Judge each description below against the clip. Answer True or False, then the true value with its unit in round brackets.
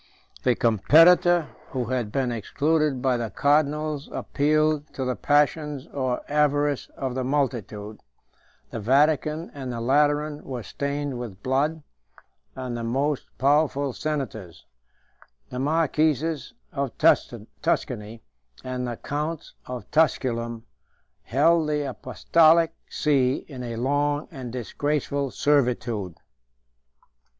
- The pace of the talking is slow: True (110 wpm)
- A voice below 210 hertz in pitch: True (140 Hz)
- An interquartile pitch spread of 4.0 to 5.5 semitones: False (3.3 semitones)